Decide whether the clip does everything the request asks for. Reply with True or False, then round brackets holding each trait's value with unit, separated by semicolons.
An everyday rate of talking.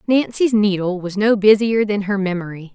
True (175 wpm)